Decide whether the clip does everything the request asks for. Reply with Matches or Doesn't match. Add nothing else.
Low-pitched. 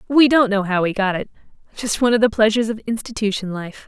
Doesn't match